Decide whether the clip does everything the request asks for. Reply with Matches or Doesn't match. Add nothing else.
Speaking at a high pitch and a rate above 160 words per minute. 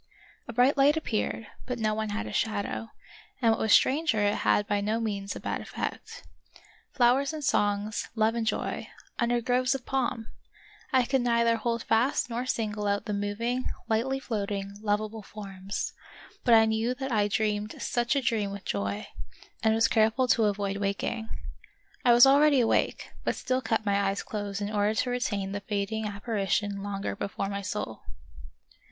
Matches